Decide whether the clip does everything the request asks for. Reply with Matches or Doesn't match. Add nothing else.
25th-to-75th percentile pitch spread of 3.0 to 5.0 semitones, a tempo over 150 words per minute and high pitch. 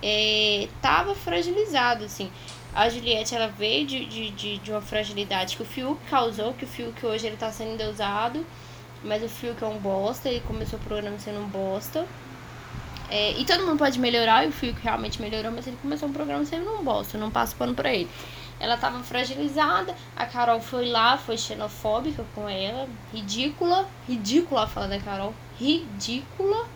Matches